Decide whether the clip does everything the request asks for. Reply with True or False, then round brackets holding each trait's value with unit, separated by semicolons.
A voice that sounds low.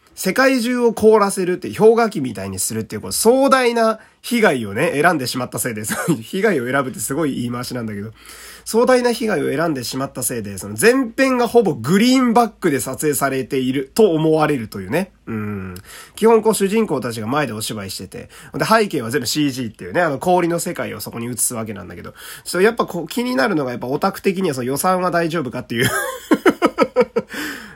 False (150 Hz)